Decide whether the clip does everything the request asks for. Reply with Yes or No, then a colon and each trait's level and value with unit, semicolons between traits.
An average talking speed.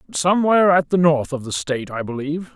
No: fast, 210 wpm